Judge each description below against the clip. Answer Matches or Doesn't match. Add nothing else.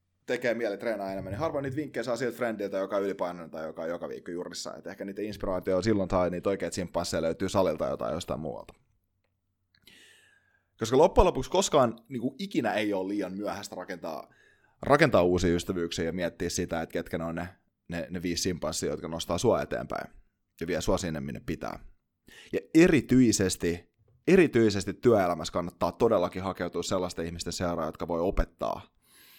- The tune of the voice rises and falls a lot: Doesn't match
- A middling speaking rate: Doesn't match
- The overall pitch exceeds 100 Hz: Doesn't match